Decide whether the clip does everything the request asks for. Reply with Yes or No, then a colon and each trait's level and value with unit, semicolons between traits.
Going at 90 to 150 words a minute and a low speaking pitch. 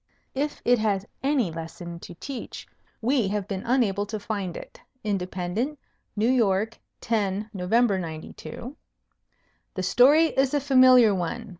No: slow, 135 wpm; high, 215 Hz